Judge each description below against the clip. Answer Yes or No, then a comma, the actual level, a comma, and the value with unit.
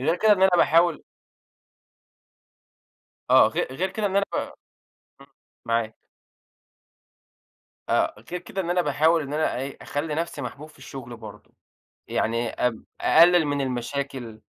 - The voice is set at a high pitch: No, medium, 145 Hz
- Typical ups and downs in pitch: No, wide, 5.7 semitones